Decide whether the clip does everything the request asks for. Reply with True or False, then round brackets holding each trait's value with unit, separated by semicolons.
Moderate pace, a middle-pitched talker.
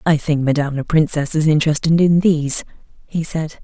True (180 wpm; 155 Hz)